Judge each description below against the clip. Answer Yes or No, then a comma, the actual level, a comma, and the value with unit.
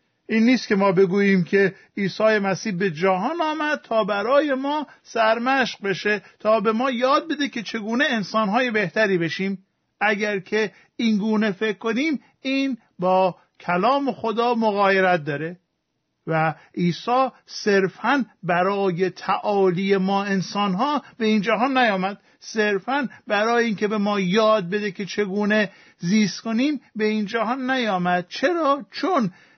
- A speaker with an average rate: Yes, average, 130 wpm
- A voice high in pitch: Yes, high, 215 Hz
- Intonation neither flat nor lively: Yes, average, 3.7 semitones